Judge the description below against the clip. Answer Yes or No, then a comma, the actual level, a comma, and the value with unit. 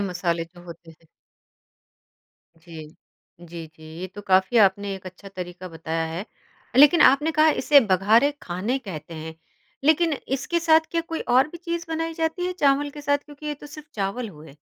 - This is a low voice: No, high, 205 Hz